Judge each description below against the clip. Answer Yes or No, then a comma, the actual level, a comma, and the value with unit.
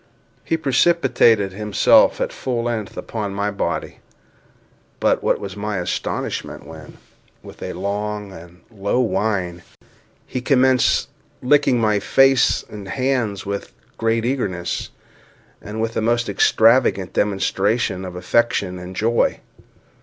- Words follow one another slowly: Yes, slow, 125 wpm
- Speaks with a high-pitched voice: No, low, 105 Hz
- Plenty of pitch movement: No, average, 3.5 semitones